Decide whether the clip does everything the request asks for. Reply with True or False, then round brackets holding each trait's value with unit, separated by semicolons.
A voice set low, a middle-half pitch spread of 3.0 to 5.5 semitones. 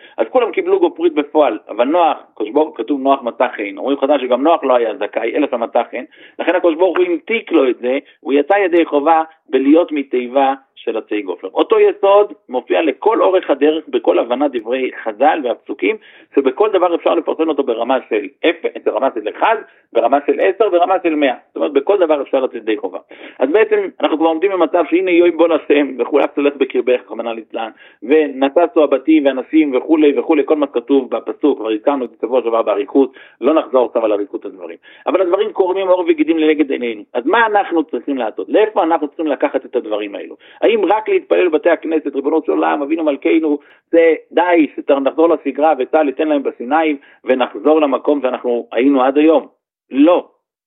False (160 Hz; 5.2 semitones)